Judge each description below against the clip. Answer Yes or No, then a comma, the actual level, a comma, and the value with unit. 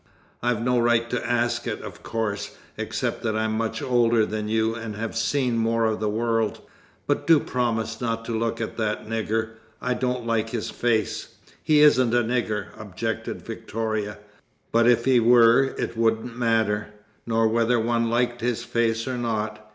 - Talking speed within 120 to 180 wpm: Yes, average, 175 wpm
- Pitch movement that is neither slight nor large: No, narrow, 1.4 semitones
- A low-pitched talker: Yes, low, 115 Hz